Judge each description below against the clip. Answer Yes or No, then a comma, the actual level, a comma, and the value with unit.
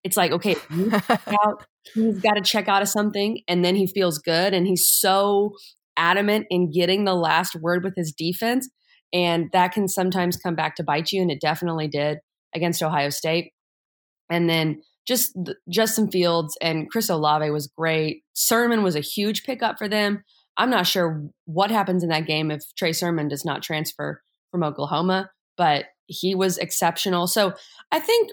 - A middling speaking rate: Yes, average, 175 wpm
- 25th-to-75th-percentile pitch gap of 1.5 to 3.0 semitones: No, average, 3.7 semitones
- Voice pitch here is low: No, medium, 180 Hz